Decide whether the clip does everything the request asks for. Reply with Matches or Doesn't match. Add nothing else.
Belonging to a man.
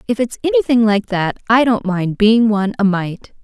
Doesn't match